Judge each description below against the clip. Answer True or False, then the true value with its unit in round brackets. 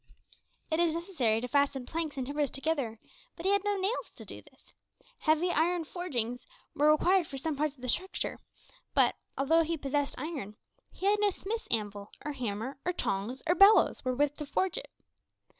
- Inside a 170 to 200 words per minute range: True (185 wpm)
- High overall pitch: True (300 Hz)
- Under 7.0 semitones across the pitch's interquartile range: True (5.1 semitones)